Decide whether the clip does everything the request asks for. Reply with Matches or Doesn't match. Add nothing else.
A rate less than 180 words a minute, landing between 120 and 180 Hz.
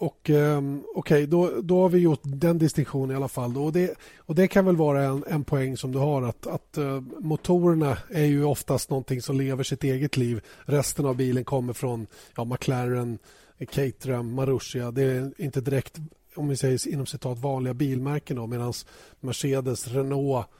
Doesn't match